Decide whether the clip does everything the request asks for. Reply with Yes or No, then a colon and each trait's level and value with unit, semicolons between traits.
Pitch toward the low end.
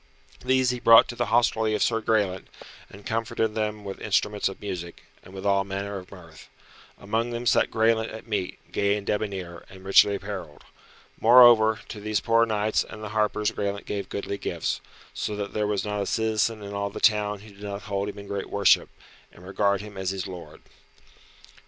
Yes: low, 105 Hz